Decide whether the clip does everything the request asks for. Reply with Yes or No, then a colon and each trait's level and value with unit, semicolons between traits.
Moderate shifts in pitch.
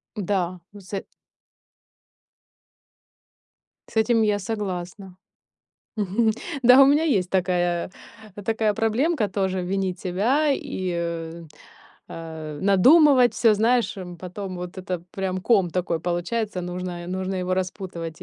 Yes: average, 3.6 semitones